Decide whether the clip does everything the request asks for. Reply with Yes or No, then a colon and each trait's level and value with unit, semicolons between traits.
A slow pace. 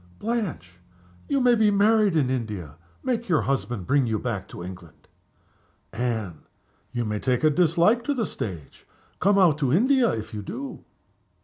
No: average, 165 wpm